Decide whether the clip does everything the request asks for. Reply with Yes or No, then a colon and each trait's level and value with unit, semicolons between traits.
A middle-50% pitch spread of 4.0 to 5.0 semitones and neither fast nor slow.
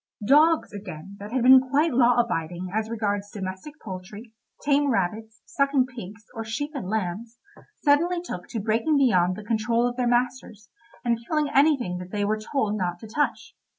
Yes: average, 4.5 semitones; average, 175 wpm